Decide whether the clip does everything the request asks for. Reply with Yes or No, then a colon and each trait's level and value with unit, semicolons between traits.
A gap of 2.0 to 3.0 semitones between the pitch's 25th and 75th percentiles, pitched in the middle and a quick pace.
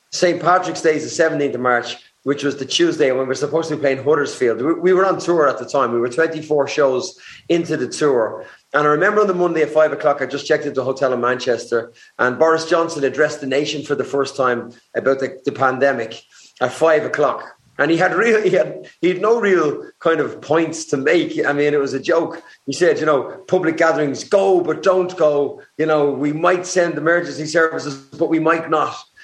No: average, 3.6 semitones; medium, 155 Hz; fast, 225 wpm